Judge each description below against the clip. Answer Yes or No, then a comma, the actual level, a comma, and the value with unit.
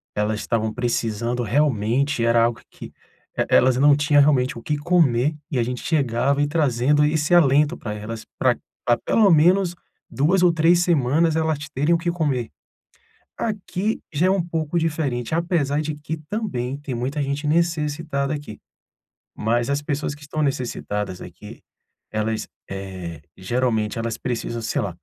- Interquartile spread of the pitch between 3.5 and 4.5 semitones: No, average, 5.0 semitones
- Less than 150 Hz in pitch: Yes, medium, 140 Hz